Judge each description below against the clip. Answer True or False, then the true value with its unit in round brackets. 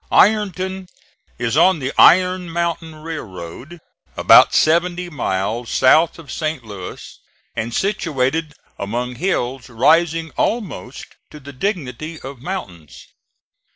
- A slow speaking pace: True (110 wpm)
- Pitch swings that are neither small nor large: False (5.8 semitones)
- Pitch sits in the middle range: True (155 Hz)